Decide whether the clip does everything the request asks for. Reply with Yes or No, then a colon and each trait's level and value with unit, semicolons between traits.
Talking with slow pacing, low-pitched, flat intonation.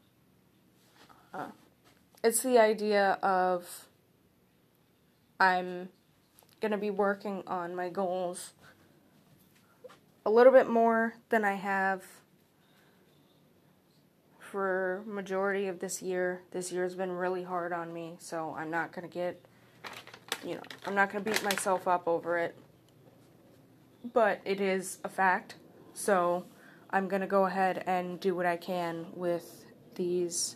No: slow, 130 wpm; medium, 185 Hz; narrow, 2.1 semitones